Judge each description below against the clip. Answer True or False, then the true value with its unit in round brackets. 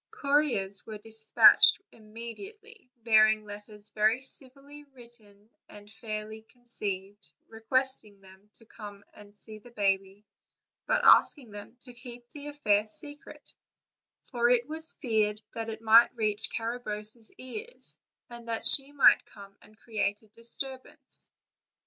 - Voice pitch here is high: True (225 Hz)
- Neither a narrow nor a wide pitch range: True (3.3 semitones)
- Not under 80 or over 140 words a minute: True (135 wpm)